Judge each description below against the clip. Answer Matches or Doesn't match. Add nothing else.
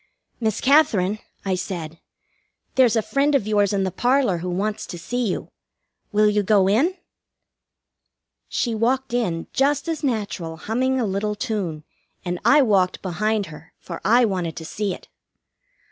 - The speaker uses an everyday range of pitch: Matches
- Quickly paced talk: Doesn't match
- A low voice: Doesn't match